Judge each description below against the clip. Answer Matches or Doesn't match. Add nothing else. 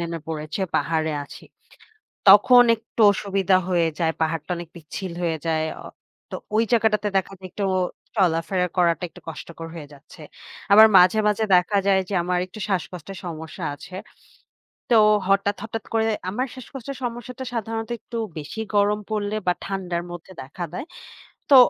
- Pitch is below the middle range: Doesn't match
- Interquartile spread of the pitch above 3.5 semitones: Matches